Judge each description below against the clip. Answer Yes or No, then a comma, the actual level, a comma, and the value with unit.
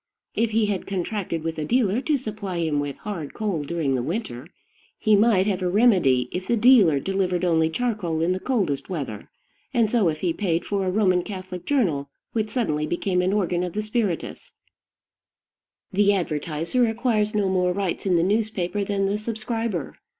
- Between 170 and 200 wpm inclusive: Yes, average, 180 wpm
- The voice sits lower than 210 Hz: Yes, high, 190 Hz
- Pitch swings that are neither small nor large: Yes, average, 4.2 semitones